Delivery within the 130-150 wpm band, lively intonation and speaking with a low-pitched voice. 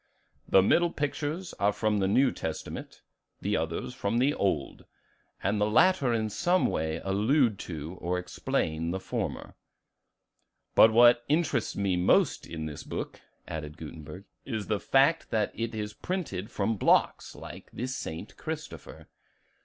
Yes: average, 145 wpm; wide, 6.5 semitones; low, 105 Hz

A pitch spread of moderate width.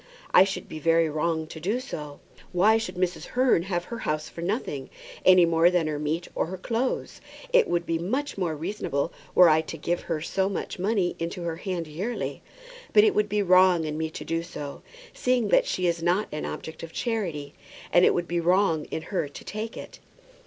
Yes: average, 3.5 semitones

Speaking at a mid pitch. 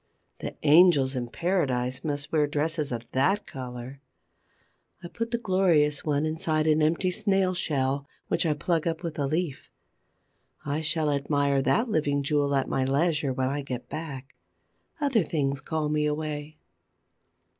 Yes: medium, 150 Hz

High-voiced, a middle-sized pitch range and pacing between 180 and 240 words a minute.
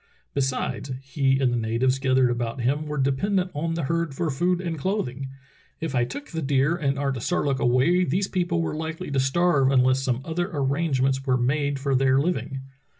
No: medium, 140 Hz; average, 4.0 semitones; average, 185 wpm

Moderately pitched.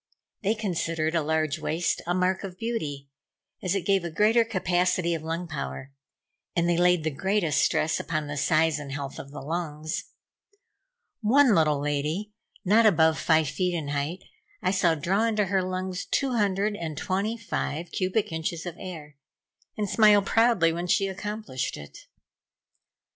Yes: medium, 175 Hz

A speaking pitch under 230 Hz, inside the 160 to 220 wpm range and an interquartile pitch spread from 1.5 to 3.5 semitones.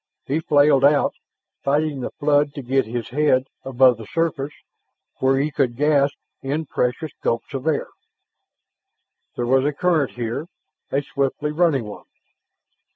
No: medium, 140 Hz; average, 145 wpm; narrow, 2.5 semitones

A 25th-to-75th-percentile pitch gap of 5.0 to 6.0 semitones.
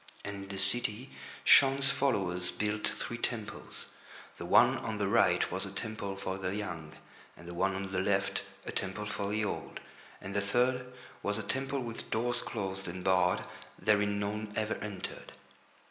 No: narrow, 2.5 semitones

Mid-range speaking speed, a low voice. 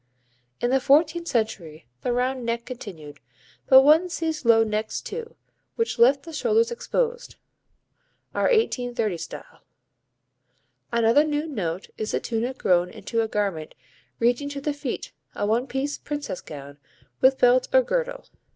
No: average, 145 wpm; very high, 255 Hz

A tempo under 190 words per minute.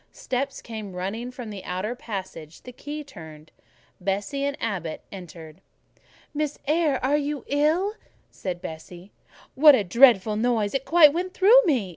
Yes: average, 150 wpm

